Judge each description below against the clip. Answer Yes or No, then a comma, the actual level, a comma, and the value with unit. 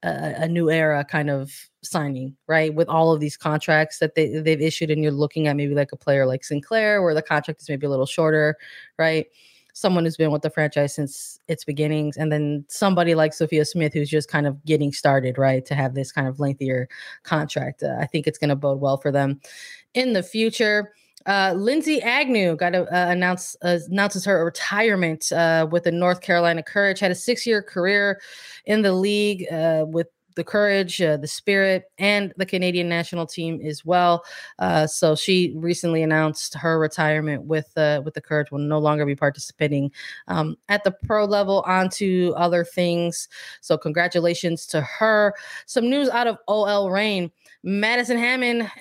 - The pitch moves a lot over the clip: No, average, 4.2 semitones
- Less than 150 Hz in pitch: No, medium, 165 Hz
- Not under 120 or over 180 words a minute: No, average, 190 wpm